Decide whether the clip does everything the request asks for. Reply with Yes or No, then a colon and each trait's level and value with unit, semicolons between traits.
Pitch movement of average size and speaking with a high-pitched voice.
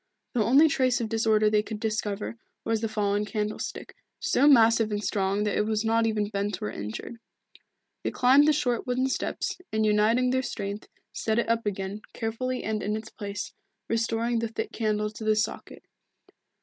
No: narrow, 1.7 semitones; high, 220 Hz